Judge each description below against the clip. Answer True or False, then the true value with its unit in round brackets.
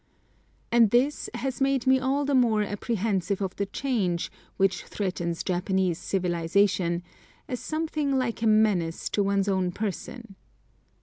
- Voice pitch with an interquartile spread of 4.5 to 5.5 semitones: True (5.0 semitones)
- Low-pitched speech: False (205 Hz)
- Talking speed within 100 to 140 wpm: True (135 wpm)